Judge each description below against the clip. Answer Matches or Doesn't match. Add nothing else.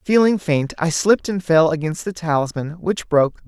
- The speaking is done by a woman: Doesn't match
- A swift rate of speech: Doesn't match